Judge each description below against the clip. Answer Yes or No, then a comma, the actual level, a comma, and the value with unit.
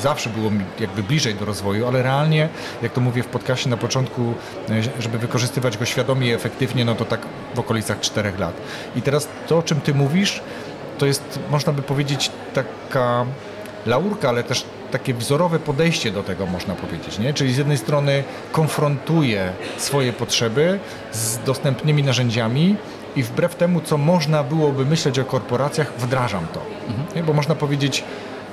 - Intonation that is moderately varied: Yes, average, 3.9 semitones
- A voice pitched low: Yes, low, 130 Hz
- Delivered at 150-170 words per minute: Yes, fast, 160 wpm